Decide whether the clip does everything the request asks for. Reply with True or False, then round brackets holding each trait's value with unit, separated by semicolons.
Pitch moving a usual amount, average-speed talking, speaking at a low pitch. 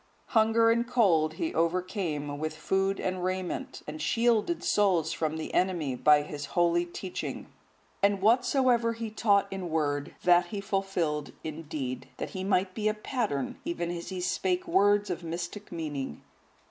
False (4.4 semitones; 160 wpm; 180 Hz)